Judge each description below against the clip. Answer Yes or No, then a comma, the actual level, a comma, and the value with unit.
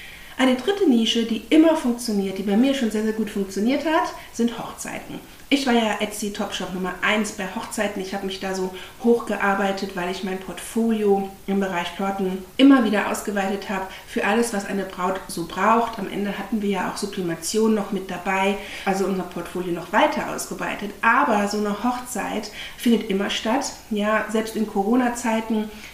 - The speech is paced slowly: No, average, 175 wpm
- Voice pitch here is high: Yes, high, 205 Hz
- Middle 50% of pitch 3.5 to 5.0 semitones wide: No, average, 2.9 semitones